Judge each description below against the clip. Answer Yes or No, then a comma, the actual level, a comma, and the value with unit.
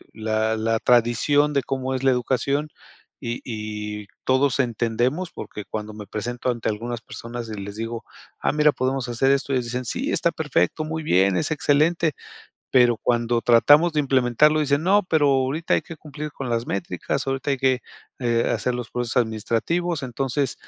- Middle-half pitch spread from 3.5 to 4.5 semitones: Yes, average, 3.9 semitones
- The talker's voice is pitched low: Yes, low, 125 Hz